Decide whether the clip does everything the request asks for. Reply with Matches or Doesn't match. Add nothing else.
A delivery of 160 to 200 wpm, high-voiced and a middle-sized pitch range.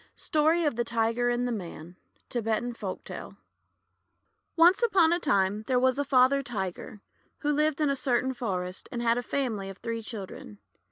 Matches